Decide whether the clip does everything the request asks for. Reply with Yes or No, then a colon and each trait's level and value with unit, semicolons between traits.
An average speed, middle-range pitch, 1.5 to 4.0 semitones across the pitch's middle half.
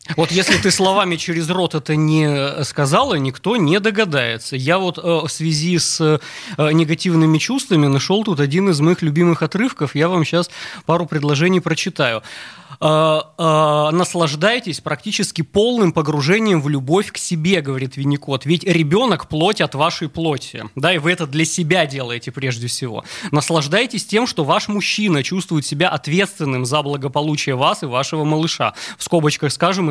Yes: average, 150 wpm; medium, 160 Hz; average, 3.4 semitones